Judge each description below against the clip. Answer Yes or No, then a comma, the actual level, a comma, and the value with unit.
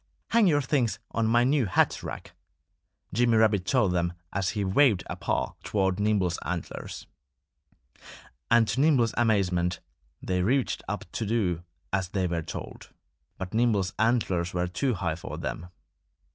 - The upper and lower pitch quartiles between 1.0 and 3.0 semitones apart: No, average, 4.8 semitones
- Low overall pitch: Yes, low, 100 Hz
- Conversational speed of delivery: Yes, average, 150 wpm